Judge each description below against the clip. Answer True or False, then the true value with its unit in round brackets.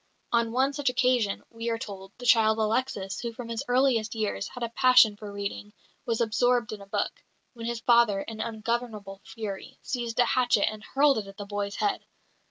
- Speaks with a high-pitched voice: True (230 Hz)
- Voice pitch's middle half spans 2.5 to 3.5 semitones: True (2.8 semitones)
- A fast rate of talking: False (195 wpm)